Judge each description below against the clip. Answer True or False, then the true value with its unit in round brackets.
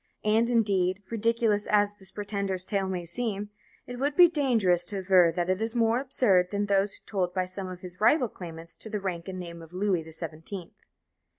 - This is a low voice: False (195 Hz)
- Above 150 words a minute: True (200 wpm)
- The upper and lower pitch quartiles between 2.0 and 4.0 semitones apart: True (3.5 semitones)